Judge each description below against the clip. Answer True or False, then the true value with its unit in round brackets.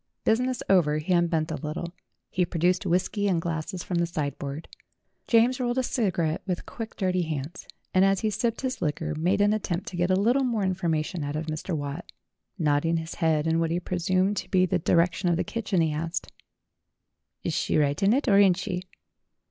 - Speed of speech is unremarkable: False (210 wpm)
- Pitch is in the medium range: True (175 Hz)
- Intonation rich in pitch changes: False (3.5 semitones)